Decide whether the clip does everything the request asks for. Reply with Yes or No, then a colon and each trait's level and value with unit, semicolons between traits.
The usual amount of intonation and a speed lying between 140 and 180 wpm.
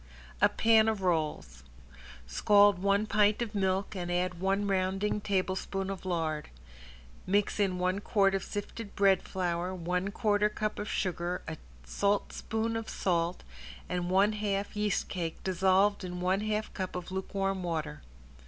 No: narrow, 2.3 semitones; average, 150 wpm